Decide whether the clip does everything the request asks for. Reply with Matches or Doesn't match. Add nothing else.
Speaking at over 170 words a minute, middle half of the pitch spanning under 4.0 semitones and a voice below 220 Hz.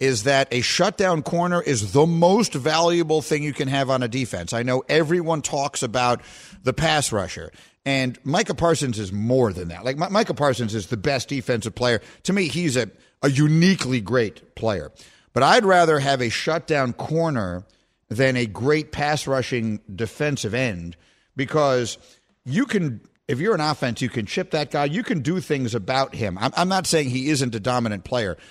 Doesn't match